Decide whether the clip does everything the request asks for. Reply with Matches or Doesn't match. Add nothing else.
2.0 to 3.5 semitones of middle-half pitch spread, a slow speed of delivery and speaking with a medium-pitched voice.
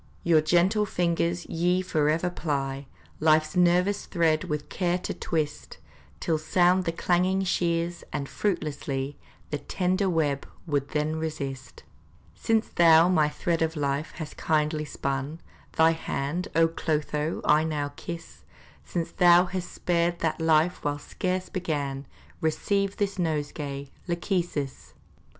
Matches